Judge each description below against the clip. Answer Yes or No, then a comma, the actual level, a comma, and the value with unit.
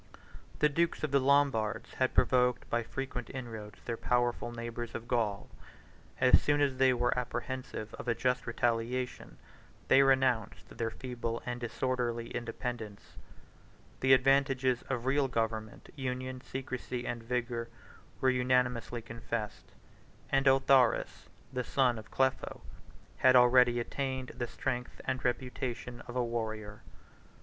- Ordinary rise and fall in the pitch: No, narrow, 1.8 semitones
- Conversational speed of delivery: No, slow, 130 wpm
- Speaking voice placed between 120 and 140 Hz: Yes, low, 125 Hz